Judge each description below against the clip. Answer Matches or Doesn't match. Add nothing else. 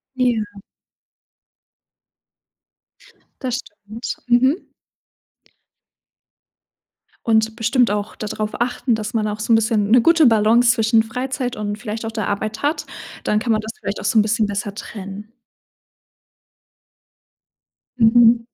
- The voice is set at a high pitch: Matches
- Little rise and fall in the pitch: Matches